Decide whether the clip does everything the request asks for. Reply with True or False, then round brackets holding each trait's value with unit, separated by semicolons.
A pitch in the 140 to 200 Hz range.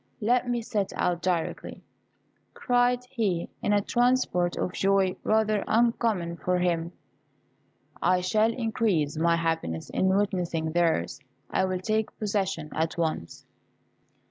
True (190 Hz)